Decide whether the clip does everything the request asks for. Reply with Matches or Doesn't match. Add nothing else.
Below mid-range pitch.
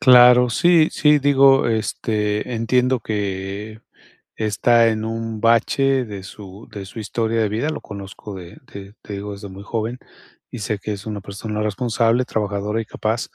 Matches